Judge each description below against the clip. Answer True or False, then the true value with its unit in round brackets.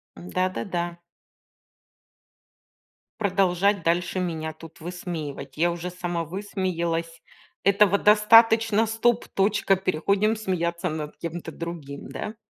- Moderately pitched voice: True (180 Hz)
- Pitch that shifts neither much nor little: True (3.2 semitones)